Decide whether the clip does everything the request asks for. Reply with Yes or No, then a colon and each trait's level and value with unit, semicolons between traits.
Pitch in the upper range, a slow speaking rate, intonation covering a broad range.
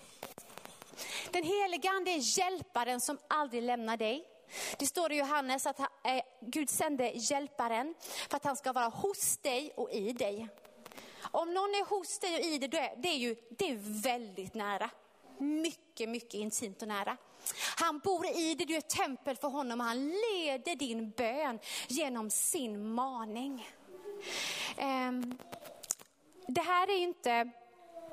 No: very high, 280 Hz; average, 155 wpm; wide, 6.0 semitones